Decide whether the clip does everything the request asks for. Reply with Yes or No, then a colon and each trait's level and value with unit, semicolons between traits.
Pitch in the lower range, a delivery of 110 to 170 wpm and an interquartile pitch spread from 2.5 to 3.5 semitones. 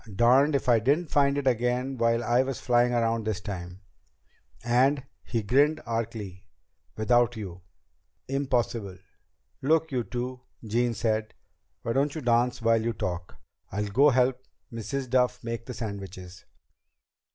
Yes: low, 120 Hz; average, 140 wpm; average, 3.0 semitones